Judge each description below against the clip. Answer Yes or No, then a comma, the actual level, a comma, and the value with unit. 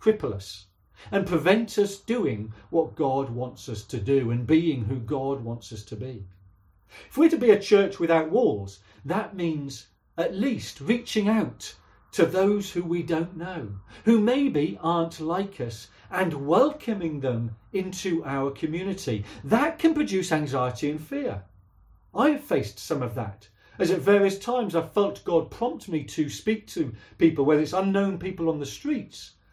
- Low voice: No, medium, 160 Hz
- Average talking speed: Yes, average, 170 wpm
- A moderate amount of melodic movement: No, wide, 9.0 semitones